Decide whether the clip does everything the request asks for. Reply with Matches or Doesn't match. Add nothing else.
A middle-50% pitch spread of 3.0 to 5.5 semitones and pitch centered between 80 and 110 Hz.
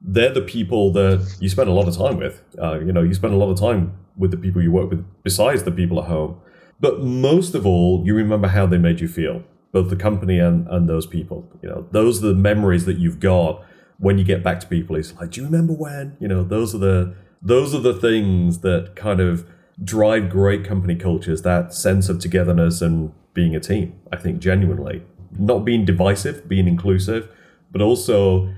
Doesn't match